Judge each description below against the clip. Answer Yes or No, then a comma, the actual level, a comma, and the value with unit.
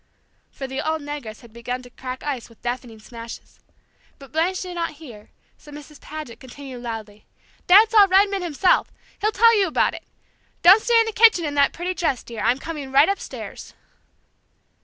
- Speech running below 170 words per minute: No, average, 180 wpm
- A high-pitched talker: Yes, very high, 290 Hz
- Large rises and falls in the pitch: Yes, wide, 6.7 semitones